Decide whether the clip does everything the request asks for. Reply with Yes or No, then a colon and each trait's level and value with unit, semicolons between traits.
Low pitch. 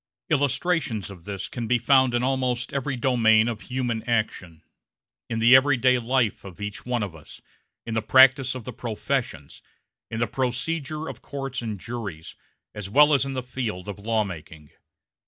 Yes: low, 120 Hz